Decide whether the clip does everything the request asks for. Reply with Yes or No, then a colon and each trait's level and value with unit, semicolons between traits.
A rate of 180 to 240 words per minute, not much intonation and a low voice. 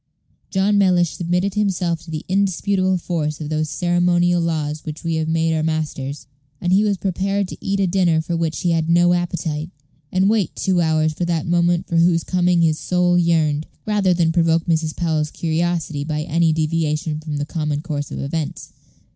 No: average, 190 wpm; narrow, 2.3 semitones; medium, 170 Hz